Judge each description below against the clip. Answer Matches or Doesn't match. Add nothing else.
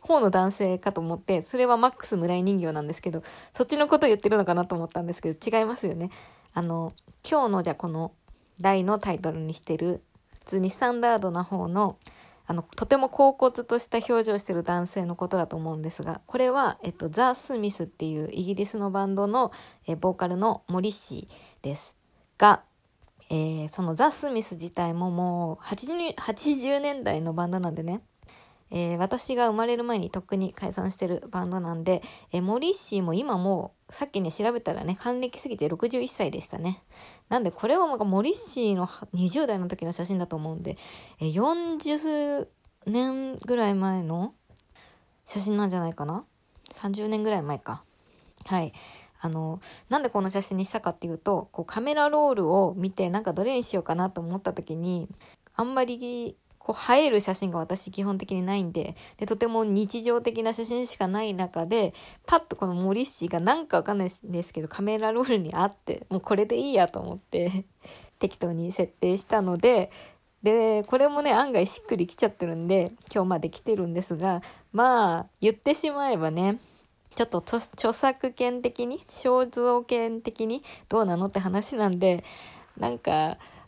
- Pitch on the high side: Matches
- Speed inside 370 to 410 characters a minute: Doesn't match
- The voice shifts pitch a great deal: Doesn't match